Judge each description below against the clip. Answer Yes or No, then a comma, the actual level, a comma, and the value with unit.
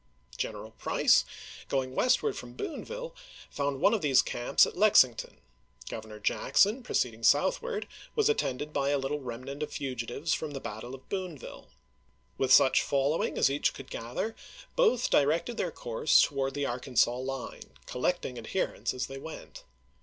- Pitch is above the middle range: No, medium, 140 Hz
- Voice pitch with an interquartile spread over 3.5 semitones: Yes, average, 5.3 semitones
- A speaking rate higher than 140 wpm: Yes, average, 155 wpm